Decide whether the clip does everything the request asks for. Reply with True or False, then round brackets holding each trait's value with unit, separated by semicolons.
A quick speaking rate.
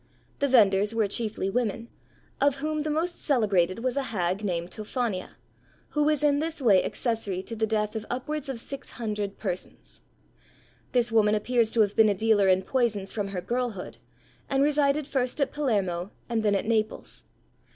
False (175 wpm)